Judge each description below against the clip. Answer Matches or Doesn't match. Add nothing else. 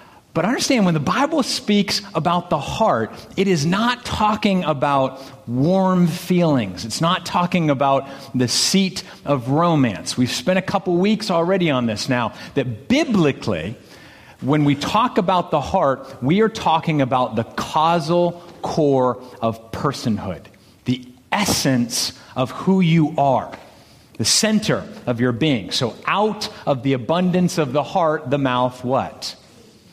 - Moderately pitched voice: Matches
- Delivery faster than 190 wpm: Doesn't match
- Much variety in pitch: Matches